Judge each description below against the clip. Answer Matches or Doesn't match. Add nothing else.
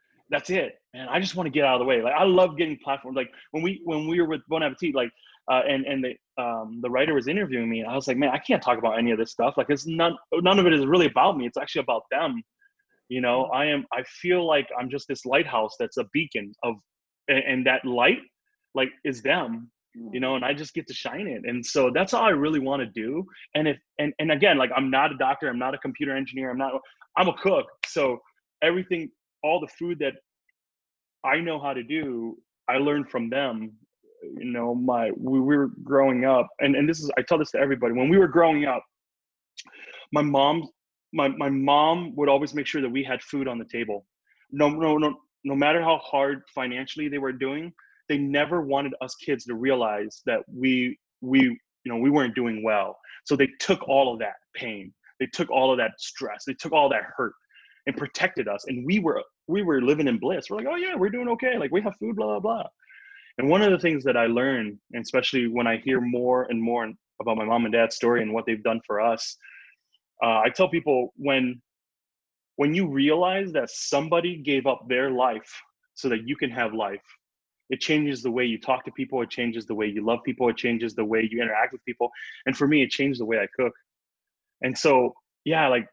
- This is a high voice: Doesn't match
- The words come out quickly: Matches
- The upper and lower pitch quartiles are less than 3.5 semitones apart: Doesn't match